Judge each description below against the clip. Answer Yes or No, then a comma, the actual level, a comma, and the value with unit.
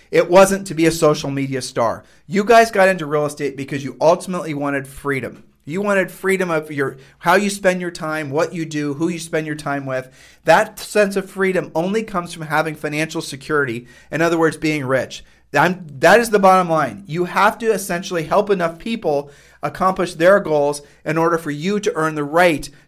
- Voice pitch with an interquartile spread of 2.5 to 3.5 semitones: No, average, 4.3 semitones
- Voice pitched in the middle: Yes, medium, 160 Hz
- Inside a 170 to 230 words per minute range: Yes, average, 200 wpm